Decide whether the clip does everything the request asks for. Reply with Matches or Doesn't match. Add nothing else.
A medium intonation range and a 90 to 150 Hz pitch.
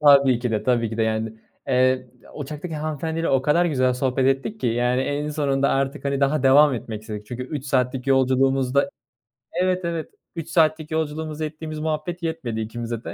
Matches